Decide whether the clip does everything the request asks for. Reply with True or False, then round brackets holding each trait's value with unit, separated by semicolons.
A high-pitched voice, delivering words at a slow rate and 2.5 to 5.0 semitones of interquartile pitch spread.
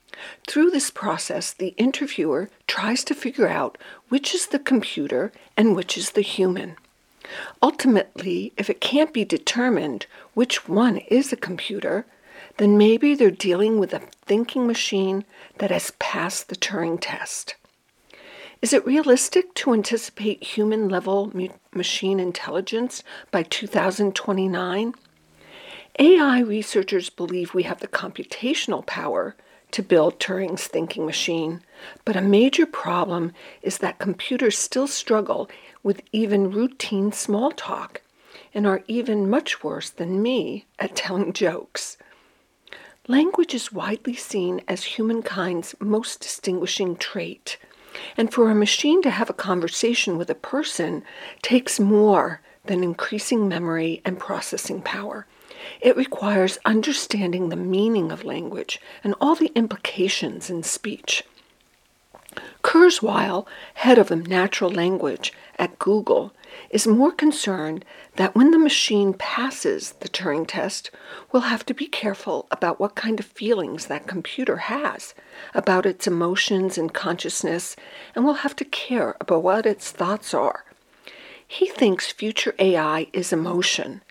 False (210 Hz; 130 wpm; 5.6 semitones)